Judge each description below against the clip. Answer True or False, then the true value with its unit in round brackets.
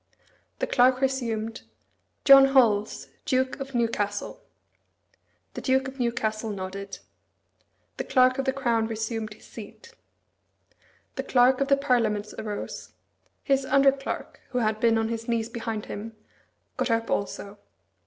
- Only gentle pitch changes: False (3.4 semitones)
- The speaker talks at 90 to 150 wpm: True (135 wpm)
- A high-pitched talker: True (235 Hz)